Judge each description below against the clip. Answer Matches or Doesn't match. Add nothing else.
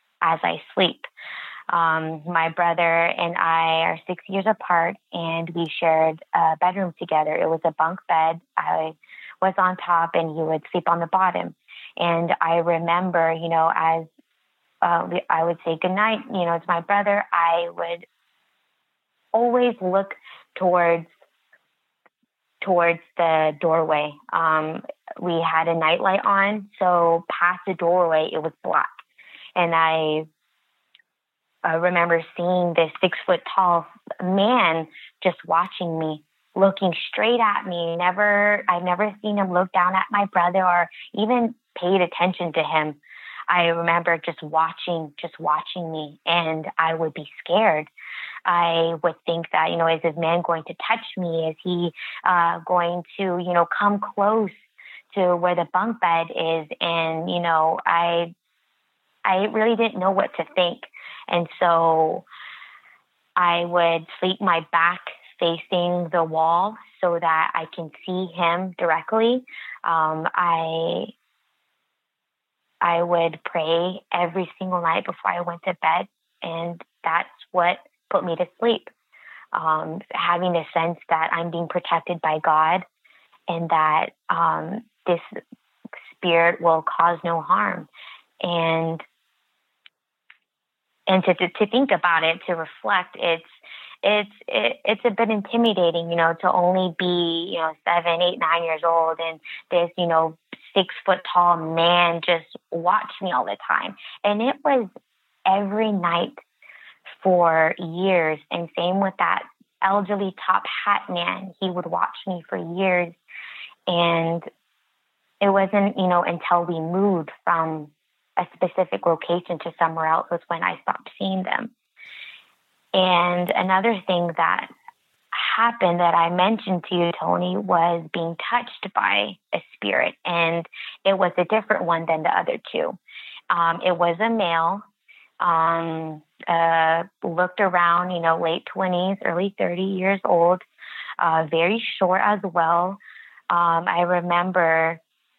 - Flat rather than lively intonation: Matches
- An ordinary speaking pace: Matches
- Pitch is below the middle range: Doesn't match